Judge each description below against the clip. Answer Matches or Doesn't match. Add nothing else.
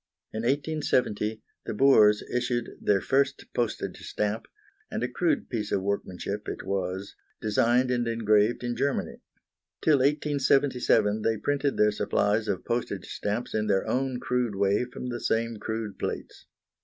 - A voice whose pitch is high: Doesn't match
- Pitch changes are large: Doesn't match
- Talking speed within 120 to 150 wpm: Matches